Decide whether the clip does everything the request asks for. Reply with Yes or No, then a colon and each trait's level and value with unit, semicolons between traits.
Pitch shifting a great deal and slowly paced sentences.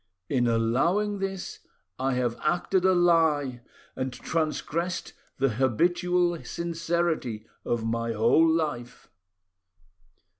Yes: wide, 6.1 semitones; slow, 100 wpm